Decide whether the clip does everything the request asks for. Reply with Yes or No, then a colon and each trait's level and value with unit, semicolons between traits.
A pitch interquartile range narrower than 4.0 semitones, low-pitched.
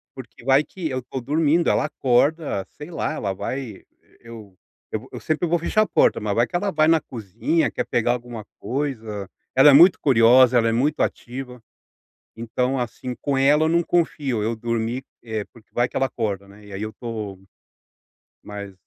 No: average, 4.7 semitones; low, 125 Hz